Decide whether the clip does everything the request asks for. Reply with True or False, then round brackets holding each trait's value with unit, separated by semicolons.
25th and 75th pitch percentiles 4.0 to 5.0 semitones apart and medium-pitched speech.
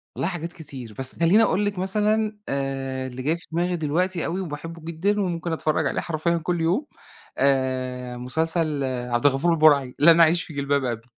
True (4.4 semitones; 160 Hz)